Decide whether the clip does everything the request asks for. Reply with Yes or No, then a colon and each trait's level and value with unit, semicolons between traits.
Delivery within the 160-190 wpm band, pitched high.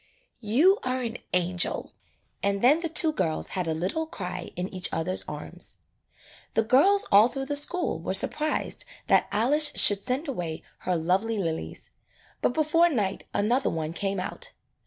Yes: average, 165 wpm; high, 225 Hz